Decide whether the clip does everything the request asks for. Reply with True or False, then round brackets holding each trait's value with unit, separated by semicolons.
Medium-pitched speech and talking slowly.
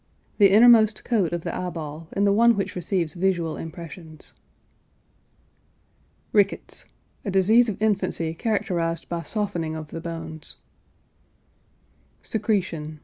True (180 Hz; 120 wpm)